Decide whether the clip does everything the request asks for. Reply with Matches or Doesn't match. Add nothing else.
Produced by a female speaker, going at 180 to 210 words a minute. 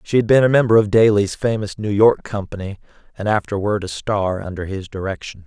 Doesn't match